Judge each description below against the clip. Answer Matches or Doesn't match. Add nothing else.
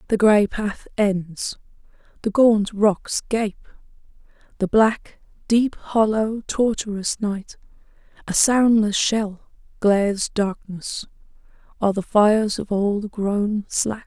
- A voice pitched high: Matches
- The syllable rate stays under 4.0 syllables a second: Matches